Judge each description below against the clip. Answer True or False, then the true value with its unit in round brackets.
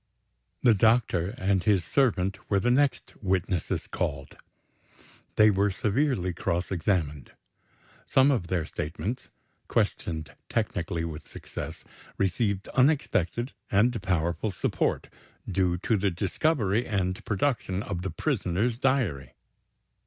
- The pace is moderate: False (115 wpm)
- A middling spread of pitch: True (4.6 semitones)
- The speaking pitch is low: True (95 Hz)